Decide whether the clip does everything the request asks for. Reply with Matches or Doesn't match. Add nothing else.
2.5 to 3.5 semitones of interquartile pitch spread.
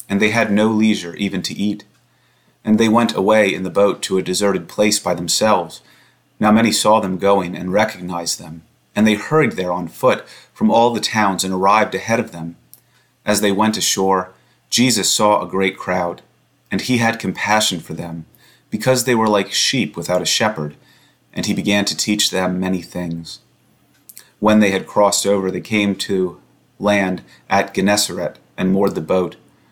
Matches